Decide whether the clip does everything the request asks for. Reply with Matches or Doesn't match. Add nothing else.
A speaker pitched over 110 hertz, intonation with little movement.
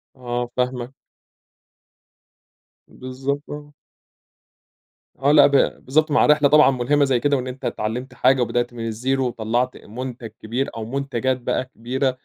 Matches